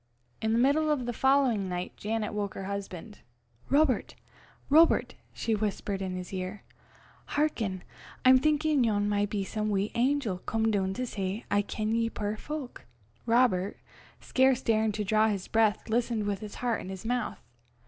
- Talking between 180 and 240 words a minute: No, average, 170 wpm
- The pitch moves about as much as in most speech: Yes, average, 3.7 semitones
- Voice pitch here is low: No, high, 220 Hz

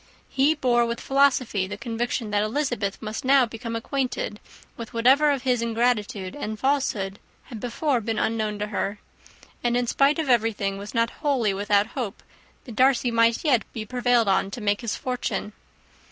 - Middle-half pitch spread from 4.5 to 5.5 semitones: No, average, 3.3 semitones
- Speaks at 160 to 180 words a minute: Yes, average, 170 wpm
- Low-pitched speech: No, high, 235 Hz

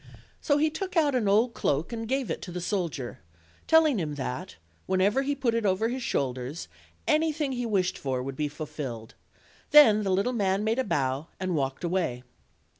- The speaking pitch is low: No, high, 195 Hz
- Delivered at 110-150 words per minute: No, average, 190 wpm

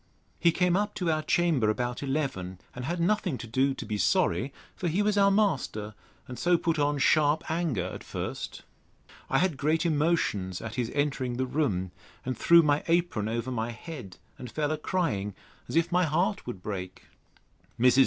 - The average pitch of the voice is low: No, medium, 145 Hz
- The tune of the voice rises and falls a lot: Yes, wide, 6.6 semitones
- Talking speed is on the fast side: No, average, 185 wpm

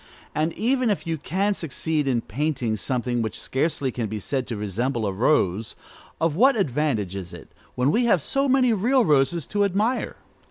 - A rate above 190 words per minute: No, average, 185 wpm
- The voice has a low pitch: No, medium, 150 Hz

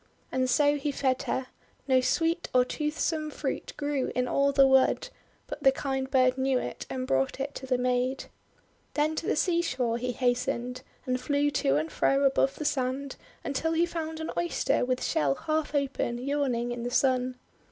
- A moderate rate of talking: Yes, average, 185 wpm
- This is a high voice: Yes, very high, 265 Hz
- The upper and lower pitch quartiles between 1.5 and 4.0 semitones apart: Yes, average, 2.7 semitones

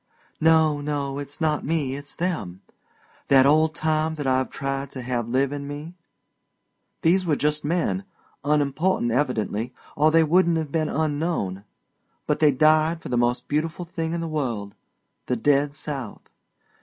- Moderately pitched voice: Yes, medium, 145 Hz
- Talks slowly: No, average, 155 wpm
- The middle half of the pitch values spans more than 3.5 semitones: No, average, 2.9 semitones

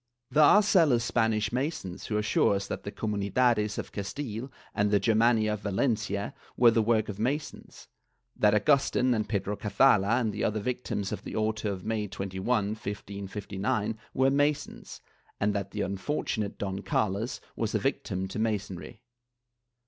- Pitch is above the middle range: No, low, 105 Hz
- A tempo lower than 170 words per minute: Yes, average, 160 wpm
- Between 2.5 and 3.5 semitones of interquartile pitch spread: Yes, average, 2.9 semitones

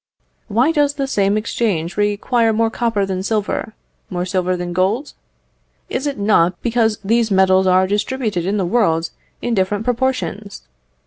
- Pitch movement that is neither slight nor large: Yes, average, 3.9 semitones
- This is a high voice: Yes, high, 210 Hz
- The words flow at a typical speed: Yes, average, 150 wpm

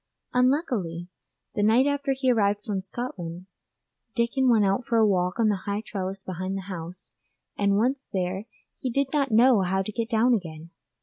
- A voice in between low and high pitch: No, high, 210 Hz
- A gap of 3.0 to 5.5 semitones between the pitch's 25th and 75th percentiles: Yes, average, 4.8 semitones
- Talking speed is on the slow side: No, average, 175 wpm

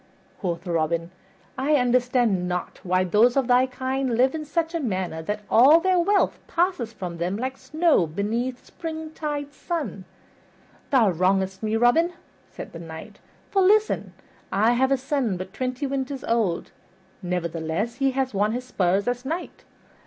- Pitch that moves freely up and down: Yes, wide, 6.7 semitones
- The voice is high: Yes, high, 245 Hz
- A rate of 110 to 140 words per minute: No, average, 160 wpm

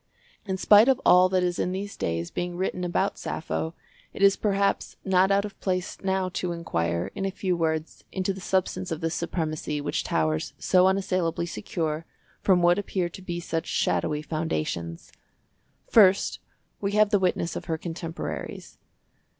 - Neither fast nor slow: Yes, average, 165 wpm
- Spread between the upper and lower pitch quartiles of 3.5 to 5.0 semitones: No, average, 2.9 semitones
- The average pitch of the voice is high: No, medium, 180 Hz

